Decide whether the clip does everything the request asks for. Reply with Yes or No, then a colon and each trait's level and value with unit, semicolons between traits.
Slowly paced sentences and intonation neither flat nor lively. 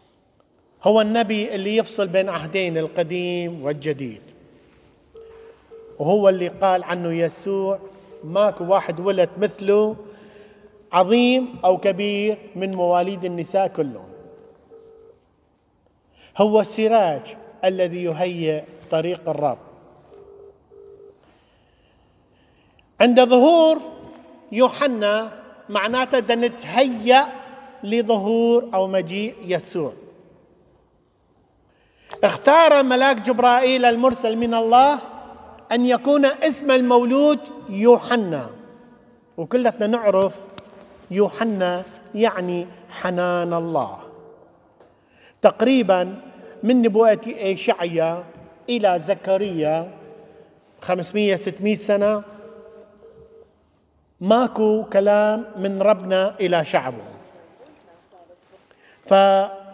Yes: slow, 70 wpm; average, 4.8 semitones